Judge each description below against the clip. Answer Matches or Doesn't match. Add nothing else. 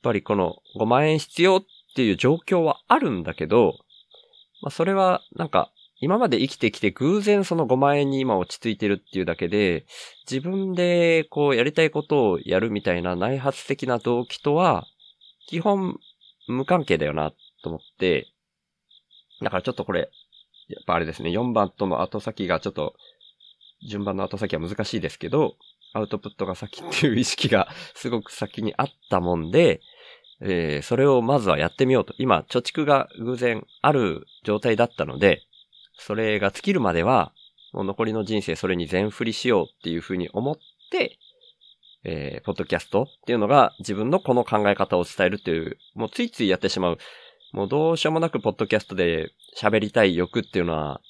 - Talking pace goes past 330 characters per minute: Matches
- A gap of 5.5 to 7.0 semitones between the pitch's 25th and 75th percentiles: Doesn't match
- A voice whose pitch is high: Doesn't match